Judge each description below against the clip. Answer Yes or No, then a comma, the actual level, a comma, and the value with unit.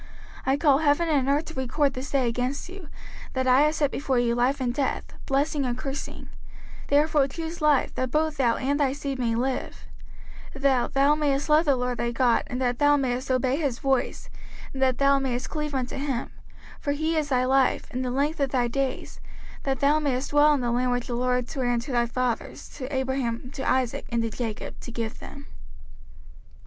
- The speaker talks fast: Yes, fast, 210 wpm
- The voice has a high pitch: Yes, very high, 265 Hz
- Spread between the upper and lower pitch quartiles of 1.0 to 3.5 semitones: Yes, narrow, 2.5 semitones